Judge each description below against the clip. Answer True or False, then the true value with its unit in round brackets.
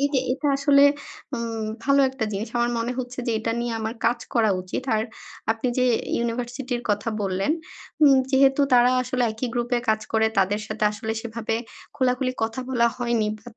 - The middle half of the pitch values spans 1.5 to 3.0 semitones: True (2.4 semitones)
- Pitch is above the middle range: True (235 Hz)